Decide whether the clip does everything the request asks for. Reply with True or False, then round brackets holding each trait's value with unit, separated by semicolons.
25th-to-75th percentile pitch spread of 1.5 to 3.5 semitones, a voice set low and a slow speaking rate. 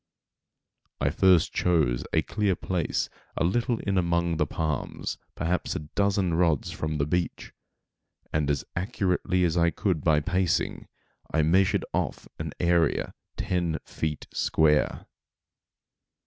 True (2.9 semitones; 85 Hz; 130 wpm)